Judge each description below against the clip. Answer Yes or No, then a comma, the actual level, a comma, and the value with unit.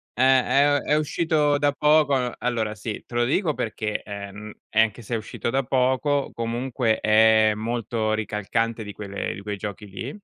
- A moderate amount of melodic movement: Yes, average, 3.7 semitones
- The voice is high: No, low, 115 Hz